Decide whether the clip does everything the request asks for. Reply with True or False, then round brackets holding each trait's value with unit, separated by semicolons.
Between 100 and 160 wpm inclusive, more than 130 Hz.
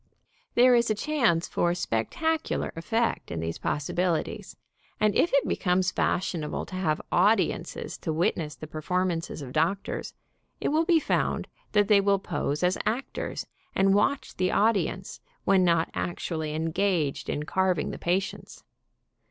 True (150 wpm; 185 Hz)